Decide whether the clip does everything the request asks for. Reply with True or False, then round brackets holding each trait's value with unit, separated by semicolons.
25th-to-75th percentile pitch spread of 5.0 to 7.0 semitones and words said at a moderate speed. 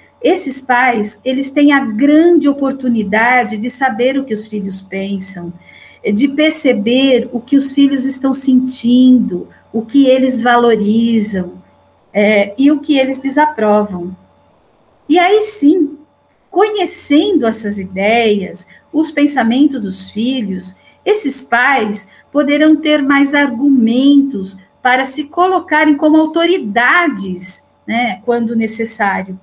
False (5.3 semitones; 115 wpm)